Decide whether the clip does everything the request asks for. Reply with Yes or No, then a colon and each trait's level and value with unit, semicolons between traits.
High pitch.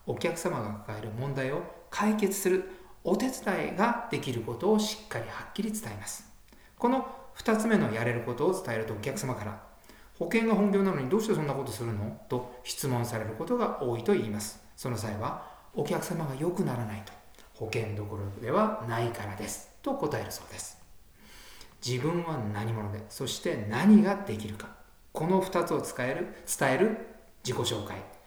No: low, 125 Hz